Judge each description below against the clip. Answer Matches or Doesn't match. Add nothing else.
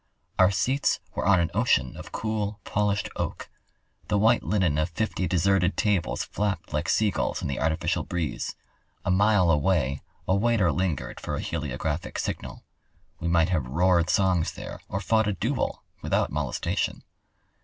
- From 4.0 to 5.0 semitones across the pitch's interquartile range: Doesn't match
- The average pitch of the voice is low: Matches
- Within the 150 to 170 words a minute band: Matches